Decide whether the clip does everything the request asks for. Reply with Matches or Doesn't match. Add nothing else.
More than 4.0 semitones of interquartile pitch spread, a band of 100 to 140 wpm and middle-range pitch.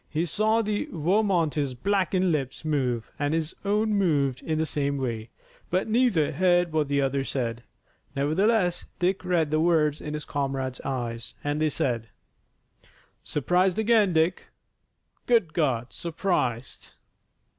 Matches